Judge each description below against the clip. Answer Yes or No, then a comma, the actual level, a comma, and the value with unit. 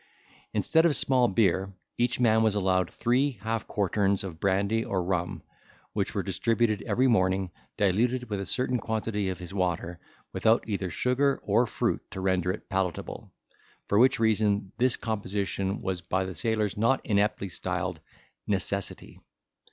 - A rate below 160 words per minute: Yes, average, 150 wpm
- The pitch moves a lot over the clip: No, average, 3.3 semitones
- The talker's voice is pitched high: No, low, 100 Hz